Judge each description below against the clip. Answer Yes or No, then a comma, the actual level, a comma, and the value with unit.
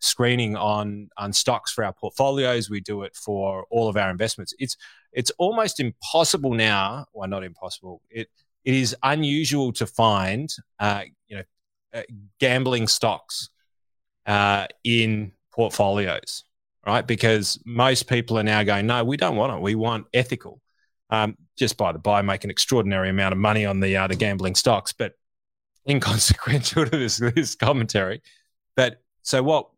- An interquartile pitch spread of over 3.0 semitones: Yes, average, 3.8 semitones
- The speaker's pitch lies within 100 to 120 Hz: Yes, low, 110 Hz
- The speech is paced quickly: No, average, 160 wpm